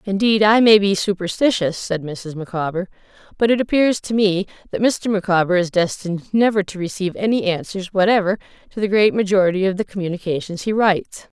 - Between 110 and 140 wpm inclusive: No, average, 175 wpm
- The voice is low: No, high, 195 Hz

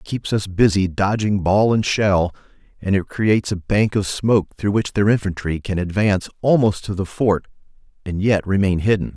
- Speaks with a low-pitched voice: Yes, low, 100 Hz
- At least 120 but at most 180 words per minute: No, average, 190 wpm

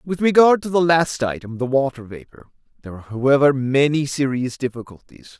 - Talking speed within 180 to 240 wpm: No, average, 145 wpm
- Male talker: Yes, male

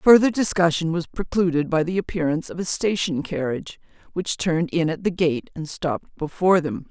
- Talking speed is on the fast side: No, average, 180 wpm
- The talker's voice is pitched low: No, medium, 170 Hz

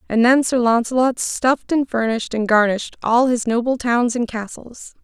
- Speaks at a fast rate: No, average, 180 wpm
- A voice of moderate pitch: No, high, 240 Hz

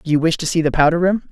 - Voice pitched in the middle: Yes, medium, 165 Hz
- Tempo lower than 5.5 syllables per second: No, 7.3 syllables/s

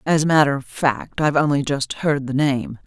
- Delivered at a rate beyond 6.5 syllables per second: No, 5.2 syllables/s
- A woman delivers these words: Yes, female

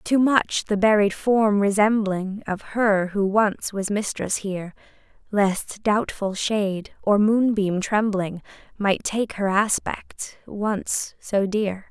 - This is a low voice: No, high, 205 Hz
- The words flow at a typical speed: No, slow, 130 wpm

